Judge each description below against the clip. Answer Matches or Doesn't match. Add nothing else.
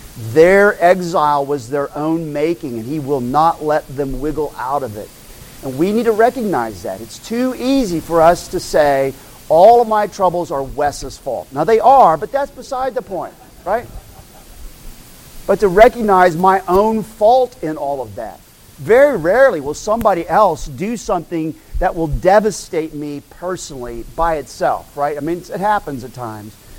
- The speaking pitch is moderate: Matches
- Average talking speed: Matches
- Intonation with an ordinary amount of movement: Doesn't match